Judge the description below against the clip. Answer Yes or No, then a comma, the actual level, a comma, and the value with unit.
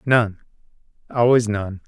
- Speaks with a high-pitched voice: No, low, 110 Hz